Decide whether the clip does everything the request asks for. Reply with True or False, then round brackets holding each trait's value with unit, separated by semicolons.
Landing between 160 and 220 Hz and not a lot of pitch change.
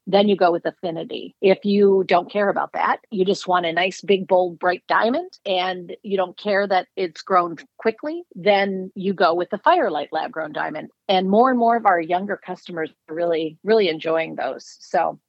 True (190 Hz; 2.3 semitones)